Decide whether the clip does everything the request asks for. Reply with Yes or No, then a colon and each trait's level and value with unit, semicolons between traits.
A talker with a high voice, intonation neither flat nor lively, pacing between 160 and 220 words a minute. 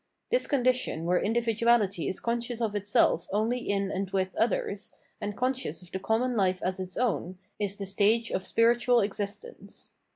Yes: high, 210 Hz; average, 3.7 semitones; average, 165 wpm